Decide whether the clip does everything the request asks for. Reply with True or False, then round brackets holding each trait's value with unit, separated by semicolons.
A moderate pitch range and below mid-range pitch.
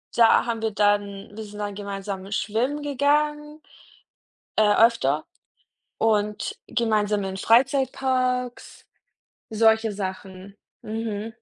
False (3.3 semitones; 220 Hz)